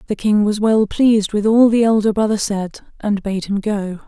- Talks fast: Yes, fast, 220 wpm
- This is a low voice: No, high, 210 Hz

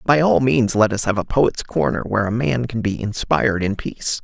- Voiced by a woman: No, male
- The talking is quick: Yes, fast, 240 wpm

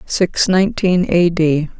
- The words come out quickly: No, slow, 135 wpm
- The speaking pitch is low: No, medium, 175 Hz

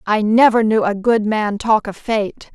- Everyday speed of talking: No, fast, 210 wpm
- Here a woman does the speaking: Yes, female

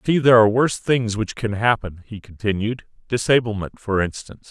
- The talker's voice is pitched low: Yes, low, 110 Hz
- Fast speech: No, average, 185 wpm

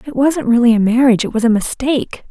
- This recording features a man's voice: No, female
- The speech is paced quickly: Yes, fast, 235 wpm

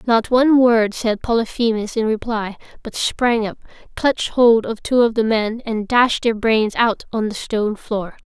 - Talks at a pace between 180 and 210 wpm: Yes, average, 190 wpm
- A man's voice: No, female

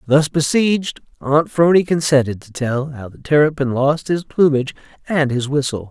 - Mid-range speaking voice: Yes, medium, 145 Hz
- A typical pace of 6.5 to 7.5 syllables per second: No, 5.0 syllables/s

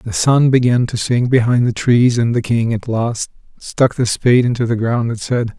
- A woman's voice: No, male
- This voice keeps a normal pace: No, fast, 225 wpm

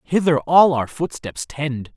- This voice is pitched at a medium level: Yes, medium, 145 Hz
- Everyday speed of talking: Yes, average, 155 wpm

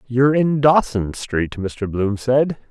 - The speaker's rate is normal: Yes, average, 155 wpm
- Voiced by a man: Yes, male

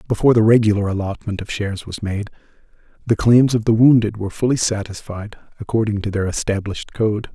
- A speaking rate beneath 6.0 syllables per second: No, 6.2 syllables/s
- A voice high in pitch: No, low, 105 Hz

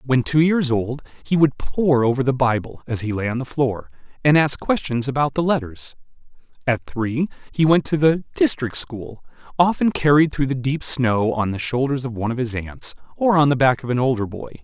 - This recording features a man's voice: Yes, male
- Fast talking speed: Yes, fast, 215 wpm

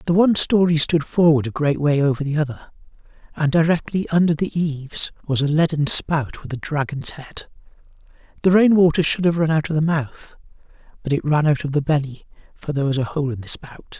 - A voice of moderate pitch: Yes, medium, 155 Hz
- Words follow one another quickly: Yes, fast, 210 wpm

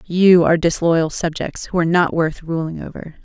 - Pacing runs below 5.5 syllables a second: Yes, 5.1 syllables/s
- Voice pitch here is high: No, medium, 170 Hz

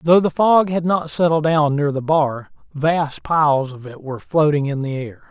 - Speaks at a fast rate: Yes, fast, 215 wpm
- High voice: No, medium, 150 Hz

